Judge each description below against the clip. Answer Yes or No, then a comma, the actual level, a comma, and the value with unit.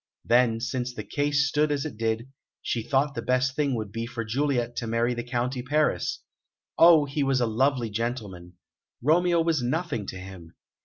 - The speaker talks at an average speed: Yes, average, 185 wpm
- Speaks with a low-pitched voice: Yes, low, 125 Hz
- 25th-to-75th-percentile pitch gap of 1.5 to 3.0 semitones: No, average, 3.9 semitones